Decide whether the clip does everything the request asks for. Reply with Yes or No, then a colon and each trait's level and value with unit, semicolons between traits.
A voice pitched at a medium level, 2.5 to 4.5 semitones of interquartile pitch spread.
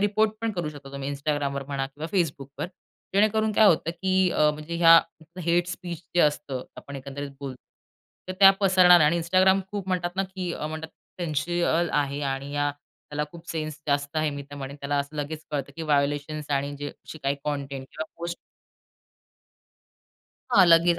Yes: medium, 155 Hz; average, 3.6 semitones